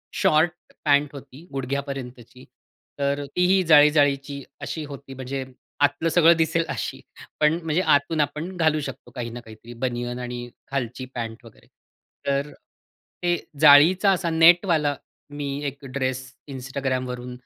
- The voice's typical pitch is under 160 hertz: Yes, medium, 140 Hz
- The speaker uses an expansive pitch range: No, average, 3.3 semitones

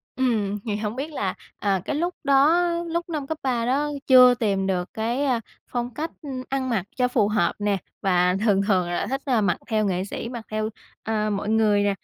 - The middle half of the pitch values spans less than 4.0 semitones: No, average, 4.5 semitones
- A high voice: Yes, high, 225 Hz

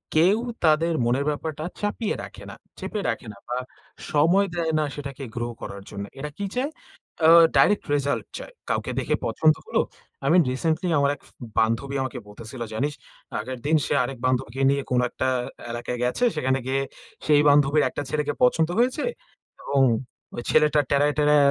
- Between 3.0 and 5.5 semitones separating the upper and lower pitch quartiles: Yes, average, 3.5 semitones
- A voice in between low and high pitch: Yes, medium, 145 Hz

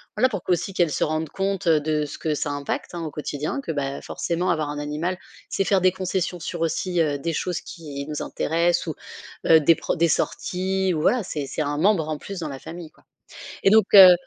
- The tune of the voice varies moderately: Yes, average, 3.4 semitones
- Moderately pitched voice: Yes, medium, 165 Hz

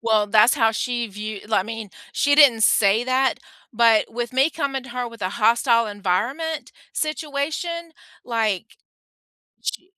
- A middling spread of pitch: Yes, average, 4.4 semitones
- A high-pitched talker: Yes, high, 235 Hz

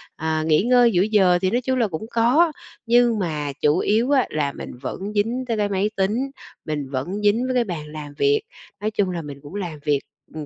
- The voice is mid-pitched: No, high, 200 Hz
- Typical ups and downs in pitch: No, wide, 7.1 semitones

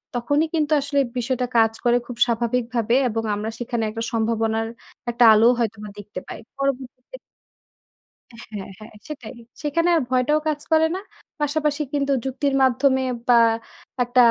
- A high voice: Yes, very high, 250 Hz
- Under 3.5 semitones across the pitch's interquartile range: No, average, 3.8 semitones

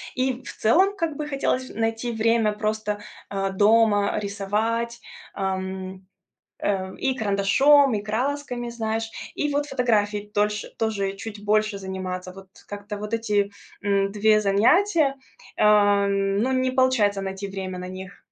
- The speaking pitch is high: Yes, high, 210 Hz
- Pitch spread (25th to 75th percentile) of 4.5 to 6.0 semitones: No, average, 3.1 semitones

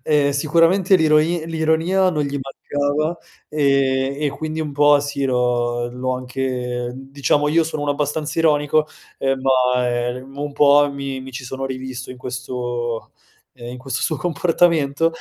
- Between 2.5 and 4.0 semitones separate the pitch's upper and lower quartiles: Yes, average, 2.9 semitones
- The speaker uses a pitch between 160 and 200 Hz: No, medium, 140 Hz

